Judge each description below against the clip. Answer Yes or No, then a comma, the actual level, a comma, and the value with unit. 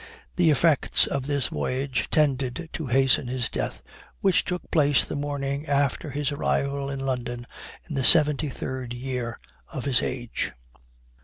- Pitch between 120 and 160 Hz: Yes, medium, 140 Hz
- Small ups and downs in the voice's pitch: Yes, narrow, 2.3 semitones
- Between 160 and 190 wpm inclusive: No, average, 145 wpm